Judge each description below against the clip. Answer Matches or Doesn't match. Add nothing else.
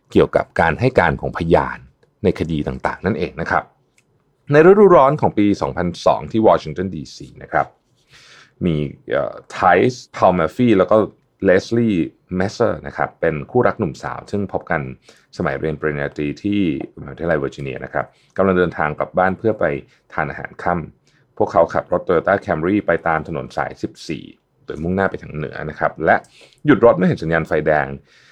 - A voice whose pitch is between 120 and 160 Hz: Doesn't match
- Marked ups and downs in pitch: Matches